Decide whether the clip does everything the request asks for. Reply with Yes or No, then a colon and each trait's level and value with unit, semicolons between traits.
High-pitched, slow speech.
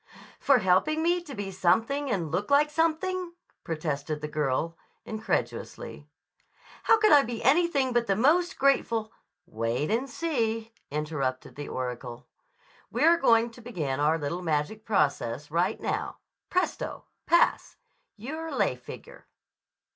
Yes: high, 225 Hz; slow, 130 wpm